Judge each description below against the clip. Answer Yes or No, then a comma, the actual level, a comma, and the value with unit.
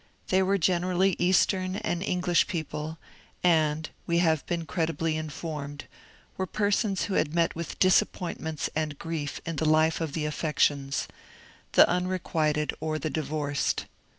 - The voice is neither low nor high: Yes, medium, 165 Hz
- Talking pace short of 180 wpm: Yes, average, 145 wpm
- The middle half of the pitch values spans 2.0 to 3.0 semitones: Yes, average, 2.7 semitones